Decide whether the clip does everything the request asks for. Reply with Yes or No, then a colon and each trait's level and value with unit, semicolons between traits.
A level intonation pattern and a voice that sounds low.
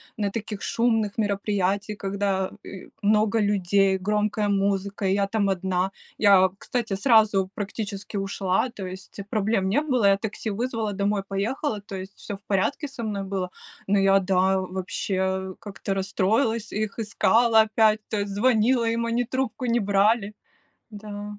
No: narrow, 2.2 semitones; high, 205 Hz